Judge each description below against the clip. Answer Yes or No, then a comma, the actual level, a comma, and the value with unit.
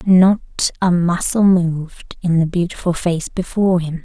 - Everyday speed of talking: Yes, average, 150 wpm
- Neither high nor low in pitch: Yes, medium, 175 Hz